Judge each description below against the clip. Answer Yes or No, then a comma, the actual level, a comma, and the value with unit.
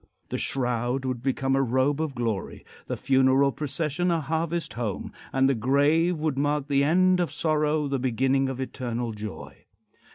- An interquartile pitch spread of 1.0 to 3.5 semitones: Yes, average, 3.0 semitones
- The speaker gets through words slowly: No, average, 165 wpm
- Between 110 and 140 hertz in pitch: Yes, low, 135 Hz